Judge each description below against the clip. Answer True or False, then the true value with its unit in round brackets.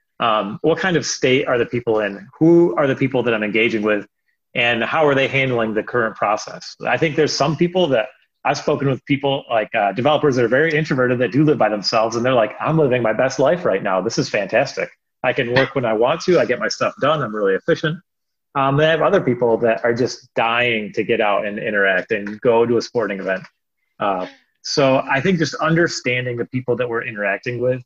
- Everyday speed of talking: False (245 wpm)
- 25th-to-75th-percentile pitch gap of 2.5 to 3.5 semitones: False (4.7 semitones)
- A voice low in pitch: True (130 Hz)